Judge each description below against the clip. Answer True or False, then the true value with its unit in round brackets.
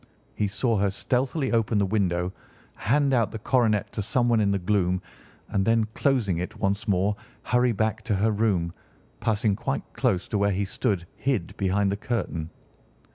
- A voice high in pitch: False (105 Hz)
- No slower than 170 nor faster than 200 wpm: True (175 wpm)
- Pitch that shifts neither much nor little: True (3.0 semitones)